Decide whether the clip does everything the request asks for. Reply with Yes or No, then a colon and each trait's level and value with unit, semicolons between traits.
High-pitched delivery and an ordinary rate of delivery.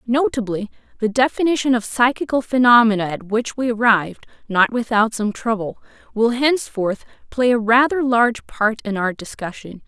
Yes: high, 230 Hz; average, 145 wpm